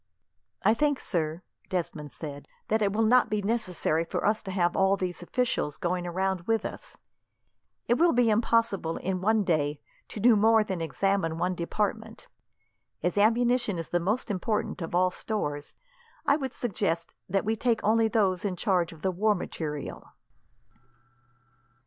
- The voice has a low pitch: No, high, 195 Hz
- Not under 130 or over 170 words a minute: Yes, average, 160 wpm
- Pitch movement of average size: Yes, average, 4.3 semitones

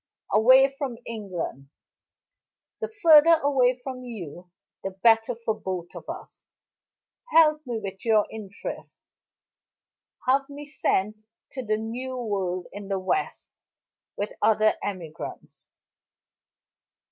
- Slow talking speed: Yes, slow, 110 wpm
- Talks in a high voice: Yes, high, 225 Hz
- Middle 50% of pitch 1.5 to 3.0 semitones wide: No, average, 4.9 semitones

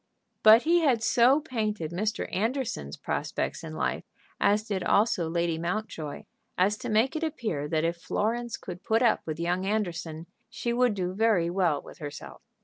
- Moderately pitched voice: No, high, 205 Hz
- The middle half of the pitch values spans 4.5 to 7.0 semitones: Yes, average, 5.1 semitones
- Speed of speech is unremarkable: Yes, average, 165 wpm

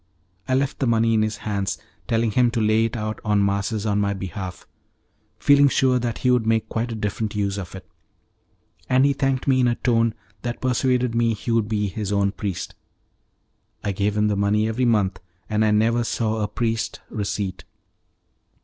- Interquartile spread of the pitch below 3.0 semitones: Yes, narrow, 2.5 semitones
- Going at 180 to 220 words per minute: Yes, average, 195 wpm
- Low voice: Yes, low, 110 Hz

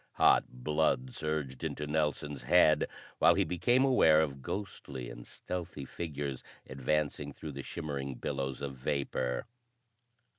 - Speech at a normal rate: No, slow, 125 wpm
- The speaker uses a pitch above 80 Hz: No, very low, 70 Hz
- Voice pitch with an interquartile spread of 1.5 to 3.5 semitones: Yes, narrow, 2.6 semitones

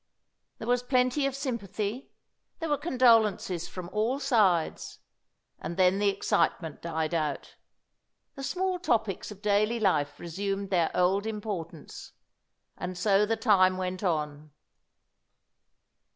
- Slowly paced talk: Yes, slow, 125 wpm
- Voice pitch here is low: No, high, 200 Hz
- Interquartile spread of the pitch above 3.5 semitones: Yes, average, 4.6 semitones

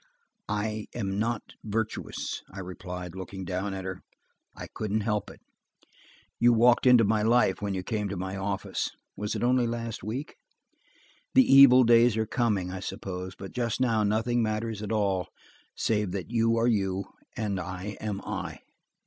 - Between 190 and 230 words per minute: No, average, 165 wpm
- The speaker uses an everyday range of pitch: Yes, average, 3.2 semitones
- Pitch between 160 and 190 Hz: No, low, 105 Hz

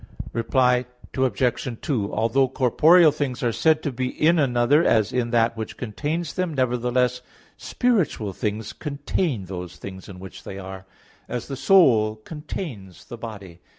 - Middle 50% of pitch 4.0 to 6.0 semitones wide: Yes, average, 5.1 semitones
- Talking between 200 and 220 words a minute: No, average, 150 wpm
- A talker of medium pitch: No, low, 125 Hz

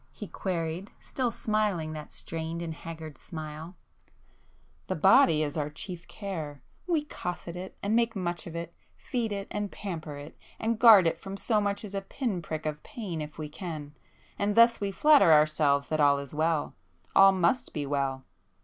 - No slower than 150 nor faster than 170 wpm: Yes, average, 165 wpm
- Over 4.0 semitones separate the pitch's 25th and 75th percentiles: Yes, average, 4.9 semitones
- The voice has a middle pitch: Yes, medium, 170 Hz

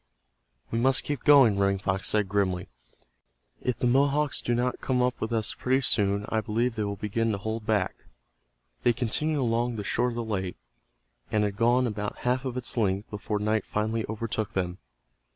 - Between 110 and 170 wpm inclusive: No, average, 190 wpm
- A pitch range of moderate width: Yes, average, 3.1 semitones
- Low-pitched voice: Yes, low, 110 Hz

